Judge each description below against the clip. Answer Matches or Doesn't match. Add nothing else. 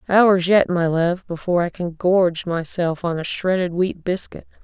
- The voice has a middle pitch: Matches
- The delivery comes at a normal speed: Matches